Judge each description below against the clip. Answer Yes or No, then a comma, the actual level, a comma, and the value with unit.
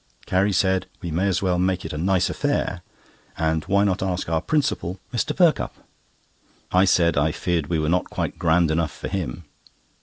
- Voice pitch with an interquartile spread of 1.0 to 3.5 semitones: Yes, average, 2.7 semitones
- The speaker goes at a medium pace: Yes, average, 185 wpm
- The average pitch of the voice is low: Yes, very low, 90 Hz